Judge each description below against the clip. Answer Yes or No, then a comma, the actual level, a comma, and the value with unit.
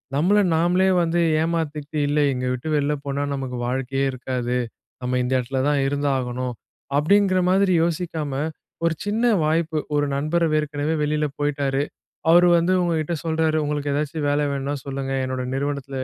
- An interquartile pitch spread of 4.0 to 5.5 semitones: No, average, 3.2 semitones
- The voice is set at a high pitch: No, medium, 145 Hz